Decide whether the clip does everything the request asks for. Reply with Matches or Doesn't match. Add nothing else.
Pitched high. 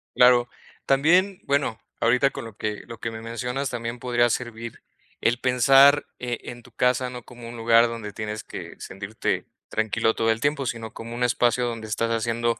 Doesn't match